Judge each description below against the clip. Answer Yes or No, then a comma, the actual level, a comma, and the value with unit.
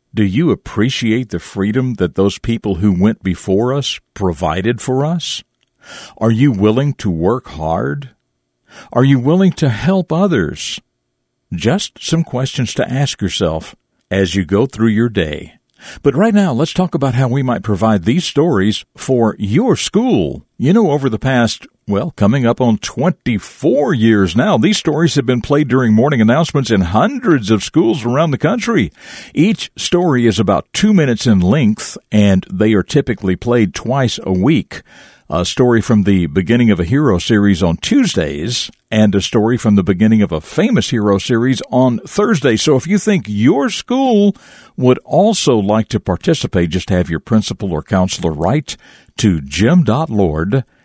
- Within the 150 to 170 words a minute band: Yes, average, 165 wpm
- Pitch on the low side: Yes, low, 115 Hz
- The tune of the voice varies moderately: No, wide, 6.0 semitones